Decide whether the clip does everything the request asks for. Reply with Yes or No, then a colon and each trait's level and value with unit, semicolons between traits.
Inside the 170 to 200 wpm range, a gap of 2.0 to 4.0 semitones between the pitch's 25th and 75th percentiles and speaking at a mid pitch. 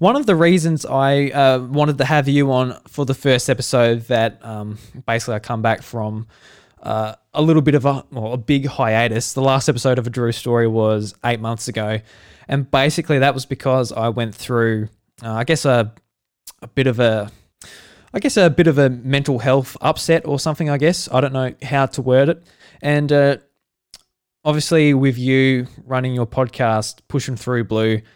No: average, 190 wpm; average, 3.6 semitones; low, 130 Hz